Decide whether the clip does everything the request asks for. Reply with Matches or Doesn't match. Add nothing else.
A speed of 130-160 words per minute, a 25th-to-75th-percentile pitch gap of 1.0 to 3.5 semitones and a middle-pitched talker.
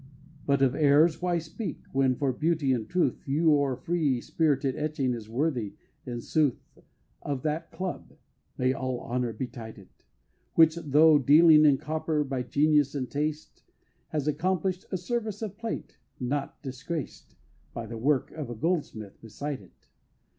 Doesn't match